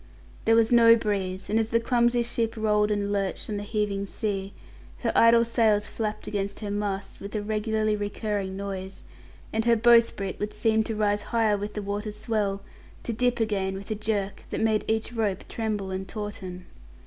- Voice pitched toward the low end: No, high, 210 Hz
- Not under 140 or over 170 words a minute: No, average, 185 wpm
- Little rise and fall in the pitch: Yes, narrow, 1.9 semitones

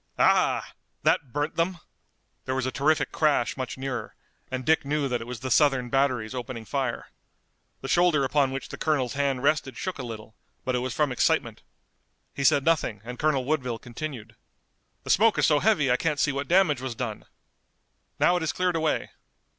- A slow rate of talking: No, average, 195 wpm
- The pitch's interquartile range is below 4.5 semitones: Yes, average, 3.5 semitones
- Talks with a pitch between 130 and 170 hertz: Yes, low, 135 Hz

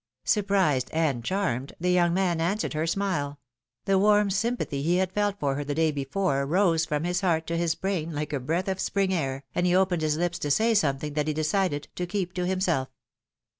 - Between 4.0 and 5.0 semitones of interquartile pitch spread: Yes, average, 4.3 semitones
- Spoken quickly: Yes, fast, 215 wpm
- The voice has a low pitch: No, medium, 170 Hz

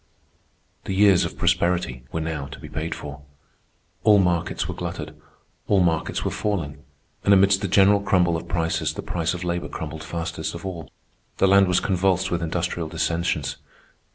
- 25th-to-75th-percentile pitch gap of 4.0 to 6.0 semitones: No, average, 2.8 semitones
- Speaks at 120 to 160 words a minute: No, average, 170 wpm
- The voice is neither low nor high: No, very low, 85 Hz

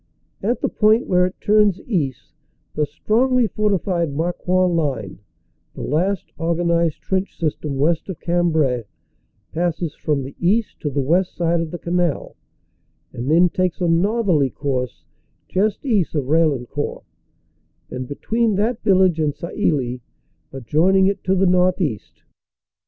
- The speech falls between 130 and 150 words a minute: Yes, average, 140 wpm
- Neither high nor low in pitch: Yes, medium, 170 Hz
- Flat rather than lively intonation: No, average, 4.4 semitones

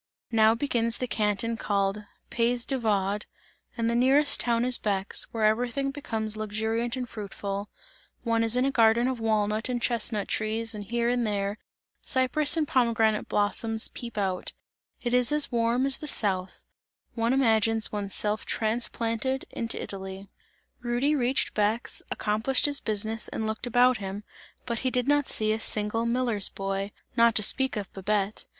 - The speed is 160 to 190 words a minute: Yes, average, 165 wpm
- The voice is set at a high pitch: Yes, high, 225 Hz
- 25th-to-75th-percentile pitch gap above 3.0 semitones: No, average, 2.7 semitones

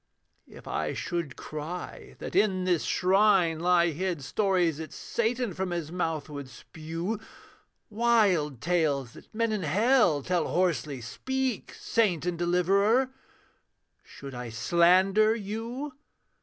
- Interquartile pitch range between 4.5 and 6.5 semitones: Yes, average, 4.9 semitones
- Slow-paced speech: Yes, slow, 125 wpm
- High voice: No, medium, 180 Hz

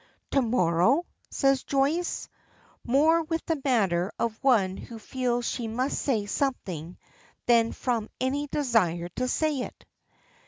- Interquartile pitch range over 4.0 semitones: Yes, average, 4.4 semitones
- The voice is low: No, high, 245 Hz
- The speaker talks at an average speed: No, slow, 130 wpm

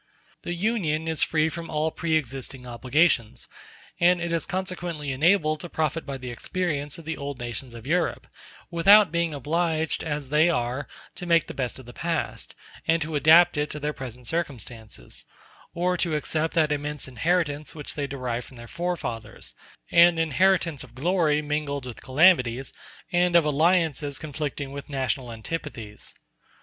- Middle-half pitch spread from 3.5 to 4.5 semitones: Yes, average, 3.9 semitones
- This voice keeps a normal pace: Yes, average, 160 wpm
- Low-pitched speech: No, medium, 150 Hz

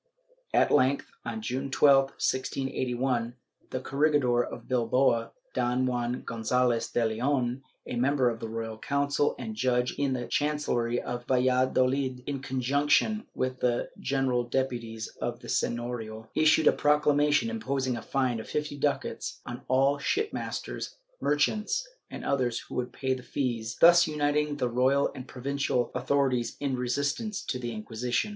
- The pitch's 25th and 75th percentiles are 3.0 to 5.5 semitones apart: No, narrow, 2.6 semitones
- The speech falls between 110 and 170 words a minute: Yes, average, 150 wpm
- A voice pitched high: No, low, 130 Hz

